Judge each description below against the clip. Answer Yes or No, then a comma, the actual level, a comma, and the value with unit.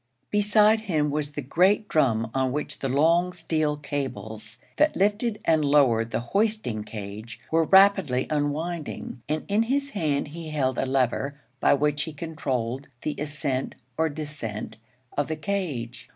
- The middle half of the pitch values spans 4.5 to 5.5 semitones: Yes, average, 4.8 semitones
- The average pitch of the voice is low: No, medium, 150 Hz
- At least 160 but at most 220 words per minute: No, average, 150 wpm